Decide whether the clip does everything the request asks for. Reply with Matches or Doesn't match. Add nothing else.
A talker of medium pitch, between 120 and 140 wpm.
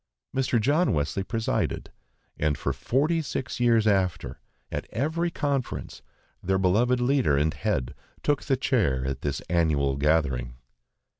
Doesn't match